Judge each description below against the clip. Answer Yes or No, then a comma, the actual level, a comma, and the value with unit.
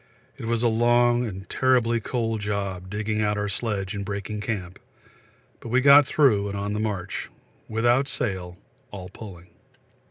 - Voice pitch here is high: No, low, 105 Hz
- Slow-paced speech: No, average, 160 wpm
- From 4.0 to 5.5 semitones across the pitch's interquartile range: No, average, 3.0 semitones